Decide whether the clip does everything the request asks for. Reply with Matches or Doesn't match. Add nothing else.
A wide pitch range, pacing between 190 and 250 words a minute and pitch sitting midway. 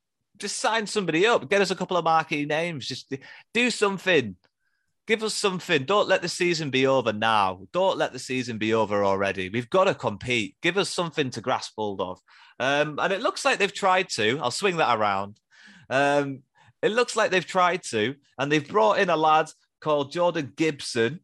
Matches